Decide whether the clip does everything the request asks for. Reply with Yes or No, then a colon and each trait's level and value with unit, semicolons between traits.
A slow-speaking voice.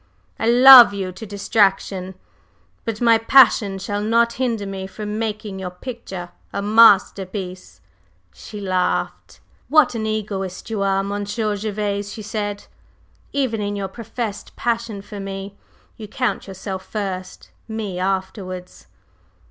Yes: slow, 130 wpm